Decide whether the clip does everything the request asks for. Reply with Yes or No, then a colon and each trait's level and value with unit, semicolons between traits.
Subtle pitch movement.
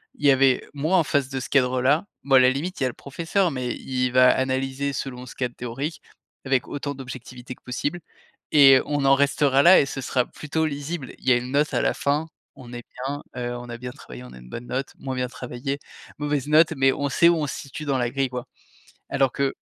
Yes: narrow, 2.3 semitones